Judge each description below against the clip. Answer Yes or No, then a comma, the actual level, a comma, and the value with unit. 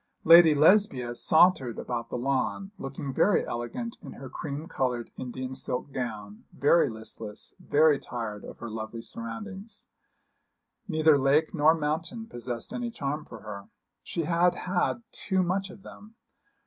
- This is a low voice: No, medium, 145 Hz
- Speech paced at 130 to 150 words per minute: Yes, average, 145 wpm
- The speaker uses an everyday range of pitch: No, wide, 6.6 semitones